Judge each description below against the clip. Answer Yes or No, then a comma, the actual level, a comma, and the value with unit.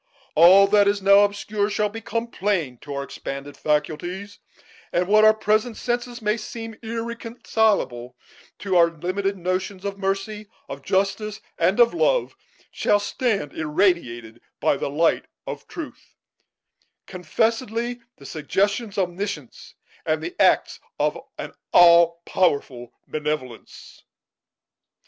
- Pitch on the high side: Yes, high, 200 Hz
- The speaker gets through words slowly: Yes, slow, 125 wpm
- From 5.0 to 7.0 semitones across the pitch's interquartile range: No, average, 4.3 semitones